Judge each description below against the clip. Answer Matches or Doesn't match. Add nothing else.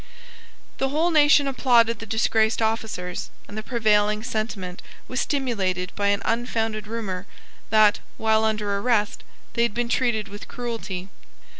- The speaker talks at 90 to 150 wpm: Matches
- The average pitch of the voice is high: Matches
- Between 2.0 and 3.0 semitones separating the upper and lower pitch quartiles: Matches